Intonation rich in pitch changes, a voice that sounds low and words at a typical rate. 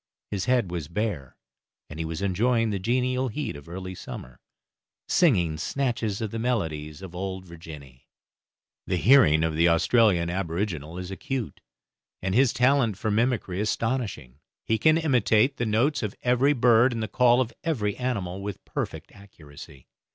Yes: wide, 6.2 semitones; low, 105 Hz; average, 160 wpm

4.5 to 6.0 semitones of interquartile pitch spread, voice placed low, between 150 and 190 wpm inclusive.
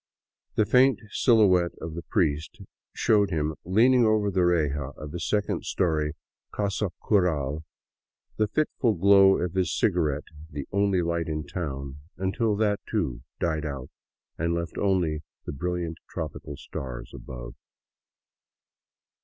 No: average, 4.9 semitones; very low, 85 Hz; slow, 135 wpm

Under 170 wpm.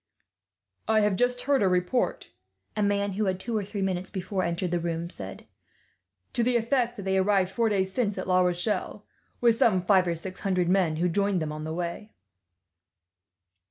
No: average, 195 wpm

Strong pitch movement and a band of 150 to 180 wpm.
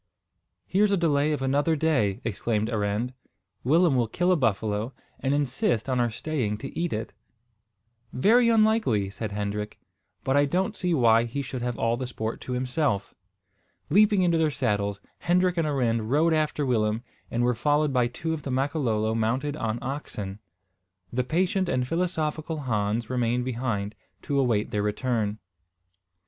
Yes: wide, 5.7 semitones; average, 160 wpm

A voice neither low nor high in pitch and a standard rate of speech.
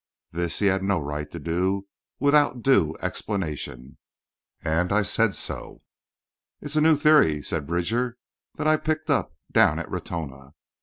No: very low, 95 Hz; average, 150 wpm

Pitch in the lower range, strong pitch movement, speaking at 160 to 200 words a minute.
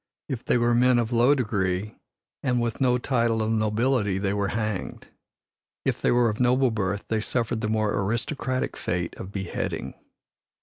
No: low, 115 Hz; average, 3.1 semitones; average, 170 wpm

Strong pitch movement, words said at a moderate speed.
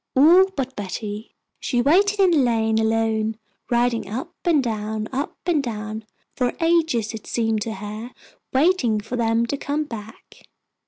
No: average, 4.6 semitones; average, 155 wpm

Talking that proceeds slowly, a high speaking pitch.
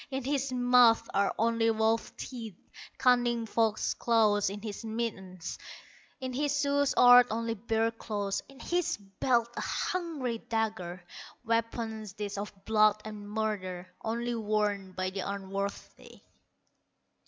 Yes: slow, 130 wpm; high, 225 Hz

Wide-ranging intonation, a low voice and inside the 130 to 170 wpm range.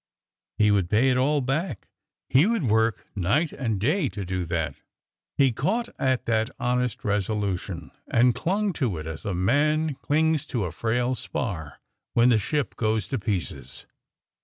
Yes: wide, 6.0 semitones; low, 115 Hz; average, 160 wpm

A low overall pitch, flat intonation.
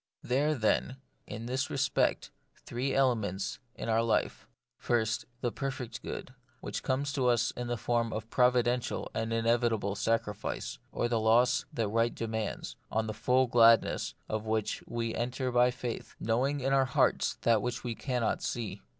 Yes: low, 120 Hz; narrow, 2.1 semitones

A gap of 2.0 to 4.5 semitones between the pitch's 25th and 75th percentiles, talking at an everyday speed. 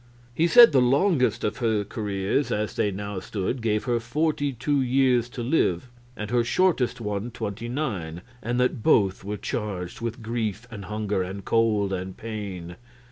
Yes: average, 3.7 semitones; average, 170 wpm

